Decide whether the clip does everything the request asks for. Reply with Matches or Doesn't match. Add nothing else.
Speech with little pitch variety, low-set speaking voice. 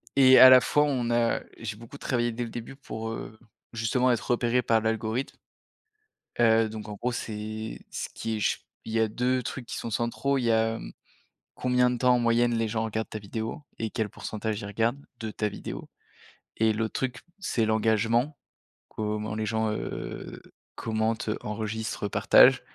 Matches